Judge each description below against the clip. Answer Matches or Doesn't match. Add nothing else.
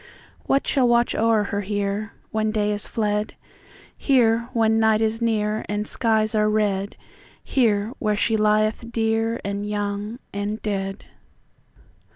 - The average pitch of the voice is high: Matches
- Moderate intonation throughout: Doesn't match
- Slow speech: Matches